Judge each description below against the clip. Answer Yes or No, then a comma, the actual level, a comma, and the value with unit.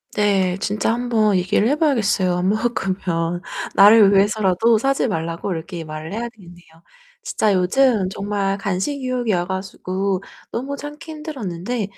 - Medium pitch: No, high, 200 Hz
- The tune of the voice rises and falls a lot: No, average, 4.5 semitones